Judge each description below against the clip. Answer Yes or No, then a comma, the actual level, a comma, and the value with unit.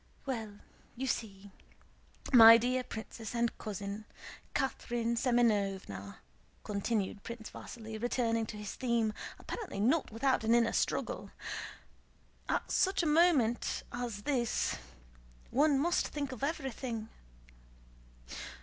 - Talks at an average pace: No, slow, 110 wpm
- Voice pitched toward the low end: No, high, 235 Hz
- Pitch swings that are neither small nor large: Yes, average, 3.1 semitones